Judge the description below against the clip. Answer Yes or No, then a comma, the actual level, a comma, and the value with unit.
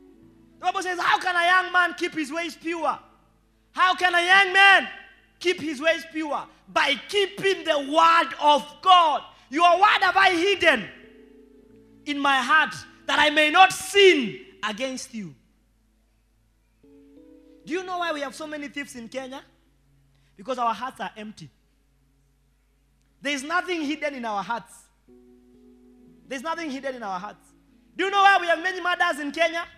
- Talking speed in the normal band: Yes, average, 165 wpm